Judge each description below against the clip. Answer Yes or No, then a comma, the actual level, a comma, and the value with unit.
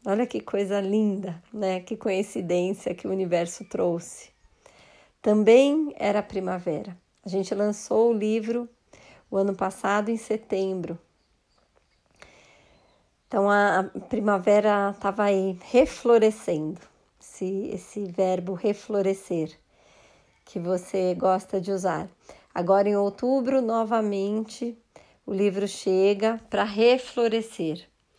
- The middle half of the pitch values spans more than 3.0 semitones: No, average, 2.7 semitones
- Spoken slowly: Yes, slow, 105 wpm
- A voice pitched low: No, high, 200 Hz